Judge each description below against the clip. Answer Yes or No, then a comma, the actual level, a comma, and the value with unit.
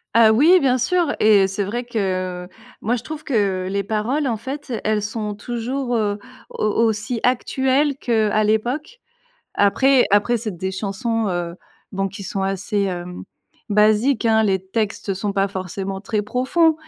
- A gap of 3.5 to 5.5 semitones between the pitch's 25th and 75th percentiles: Yes, average, 3.8 semitones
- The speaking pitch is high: Yes, high, 215 Hz